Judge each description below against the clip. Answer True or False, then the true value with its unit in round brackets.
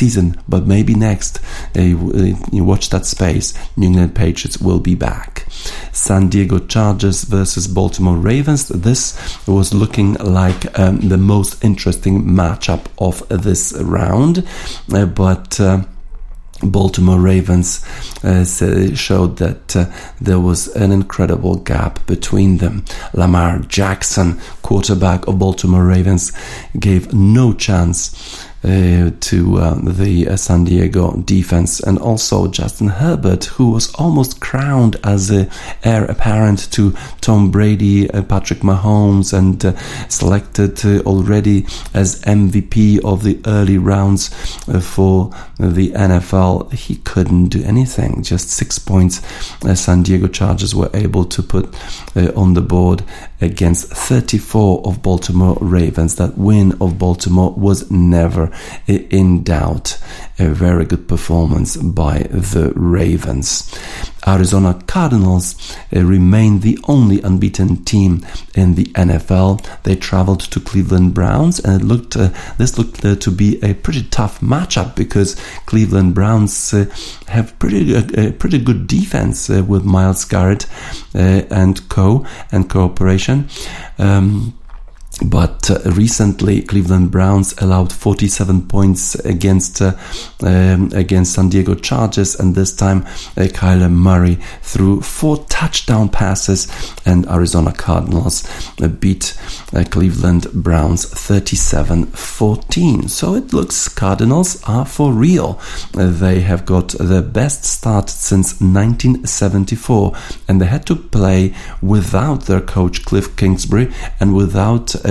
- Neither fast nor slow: False (130 wpm)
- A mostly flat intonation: True (2.2 semitones)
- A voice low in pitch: True (95 Hz)